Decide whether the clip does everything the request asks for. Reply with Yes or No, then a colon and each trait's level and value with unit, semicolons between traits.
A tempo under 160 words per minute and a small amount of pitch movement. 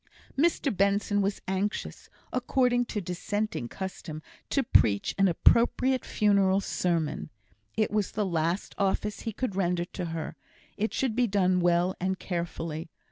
No: average, 140 wpm; average, 3.6 semitones